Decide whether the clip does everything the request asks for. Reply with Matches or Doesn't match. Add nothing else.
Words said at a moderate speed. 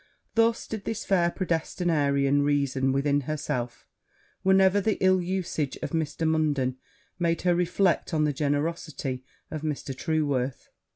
Doesn't match